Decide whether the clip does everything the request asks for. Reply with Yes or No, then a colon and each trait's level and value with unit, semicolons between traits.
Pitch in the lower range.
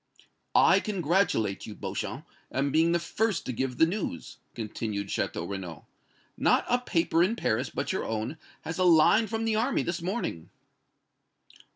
No: medium, 165 Hz